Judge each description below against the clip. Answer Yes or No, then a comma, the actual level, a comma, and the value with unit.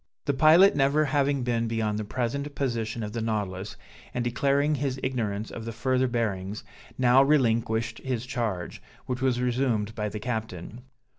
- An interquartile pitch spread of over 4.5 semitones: No, average, 3.2 semitones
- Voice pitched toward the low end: Yes, low, 120 Hz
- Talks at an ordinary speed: Yes, average, 160 wpm